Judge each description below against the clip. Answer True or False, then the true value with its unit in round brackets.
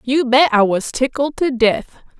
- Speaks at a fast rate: False (190 wpm)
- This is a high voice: True (255 Hz)